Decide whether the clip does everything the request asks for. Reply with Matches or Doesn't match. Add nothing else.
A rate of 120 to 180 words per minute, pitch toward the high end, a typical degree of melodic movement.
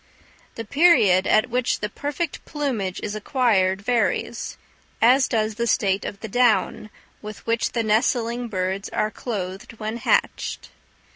Matches